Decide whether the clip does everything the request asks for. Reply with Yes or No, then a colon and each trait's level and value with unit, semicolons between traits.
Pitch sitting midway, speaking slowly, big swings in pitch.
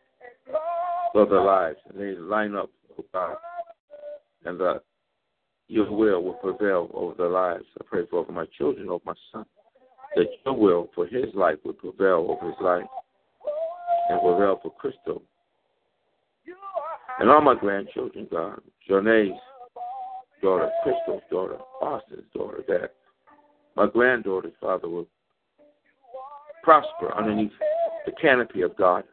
No: very high, 325 Hz; slow, 130 wpm; wide, 7.6 semitones